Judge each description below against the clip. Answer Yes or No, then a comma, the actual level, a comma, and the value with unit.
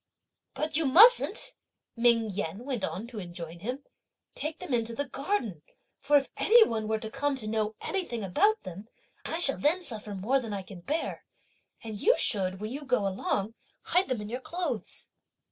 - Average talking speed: Yes, average, 185 wpm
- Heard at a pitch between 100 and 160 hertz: No, high, 235 Hz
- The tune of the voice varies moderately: No, wide, 5.9 semitones